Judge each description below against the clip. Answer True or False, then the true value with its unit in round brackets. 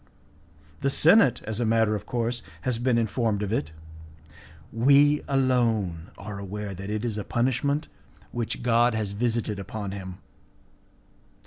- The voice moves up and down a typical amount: True (3.1 semitones)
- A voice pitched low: True (115 Hz)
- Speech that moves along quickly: False (140 wpm)